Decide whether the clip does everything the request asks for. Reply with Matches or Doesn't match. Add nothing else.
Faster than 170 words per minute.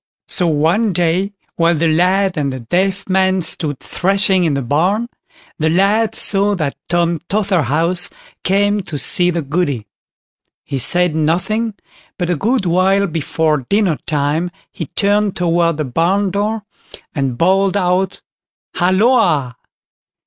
Doesn't match